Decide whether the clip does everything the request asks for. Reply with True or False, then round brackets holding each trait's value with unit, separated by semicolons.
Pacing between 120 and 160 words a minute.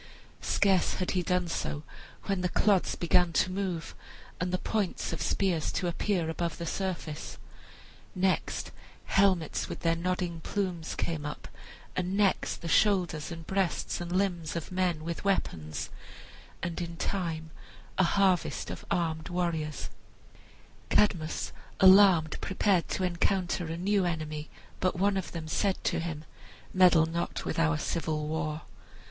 True (145 wpm)